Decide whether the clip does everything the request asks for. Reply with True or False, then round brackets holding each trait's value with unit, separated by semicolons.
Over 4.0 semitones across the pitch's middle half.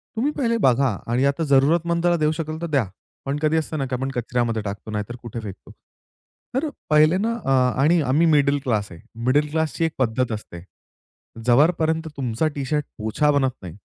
True (4.9 semitones)